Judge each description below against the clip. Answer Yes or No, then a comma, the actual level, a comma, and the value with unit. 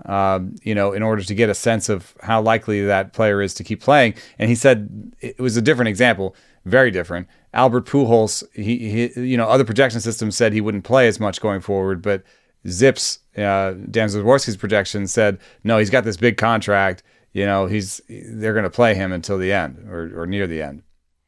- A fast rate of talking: Yes, fast, 210 wpm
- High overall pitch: No, low, 105 Hz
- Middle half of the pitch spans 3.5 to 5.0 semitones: No, average, 3.1 semitones